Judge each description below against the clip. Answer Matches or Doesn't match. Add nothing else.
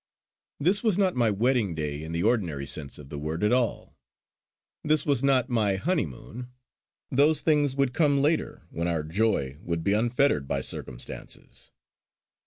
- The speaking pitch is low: Matches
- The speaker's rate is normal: Matches